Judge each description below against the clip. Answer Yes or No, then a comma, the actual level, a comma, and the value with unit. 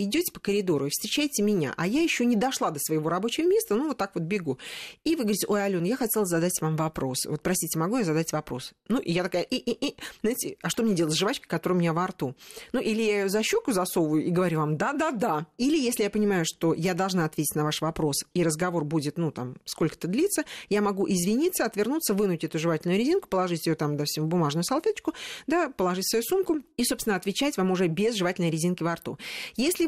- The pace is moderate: No, fast, 235 wpm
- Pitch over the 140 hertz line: Yes, high, 190 Hz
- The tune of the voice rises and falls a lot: Yes, wide, 6.6 semitones